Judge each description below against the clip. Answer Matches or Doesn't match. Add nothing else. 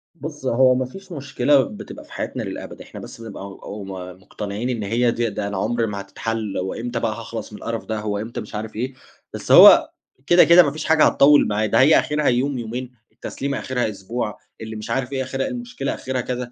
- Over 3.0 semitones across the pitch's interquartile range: Matches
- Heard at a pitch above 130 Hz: Doesn't match